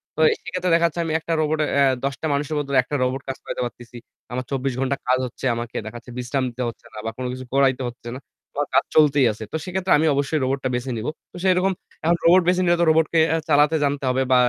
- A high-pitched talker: No, medium, 140 Hz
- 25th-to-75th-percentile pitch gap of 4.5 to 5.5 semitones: No, average, 3.9 semitones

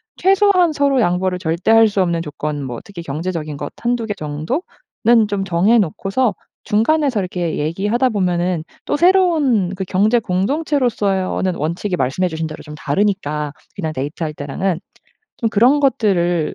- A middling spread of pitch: No, wide, 6.1 semitones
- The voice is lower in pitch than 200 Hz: Yes, high, 190 Hz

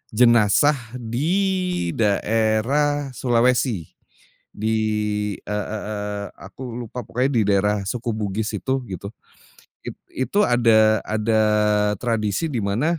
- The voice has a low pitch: Yes, low, 115 Hz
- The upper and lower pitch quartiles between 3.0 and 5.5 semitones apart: Yes, average, 3.8 semitones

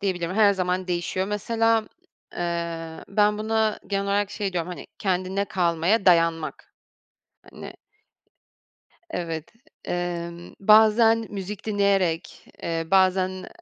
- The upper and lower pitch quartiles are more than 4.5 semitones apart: No, average, 3.2 semitones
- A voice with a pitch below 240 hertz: Yes, high, 190 Hz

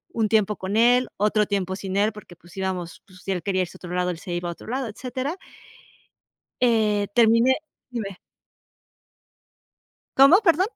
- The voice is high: Yes, high, 210 Hz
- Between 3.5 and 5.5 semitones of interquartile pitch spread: Yes, average, 4.2 semitones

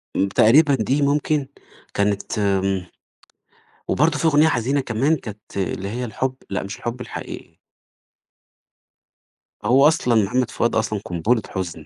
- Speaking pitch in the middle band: No, low, 120 Hz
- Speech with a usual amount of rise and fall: No, wide, 5.7 semitones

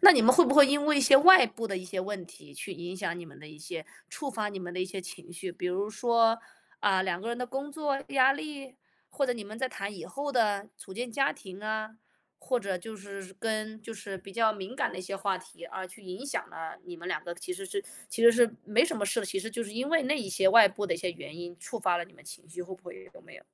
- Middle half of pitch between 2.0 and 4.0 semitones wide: No, average, 5.2 semitones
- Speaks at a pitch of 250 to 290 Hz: No, high, 205 Hz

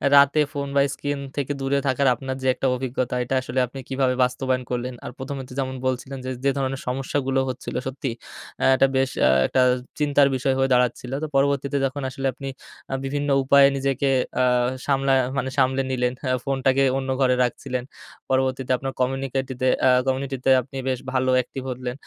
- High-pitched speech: No, low, 135 Hz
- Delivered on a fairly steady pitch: Yes, narrow, 1.1 semitones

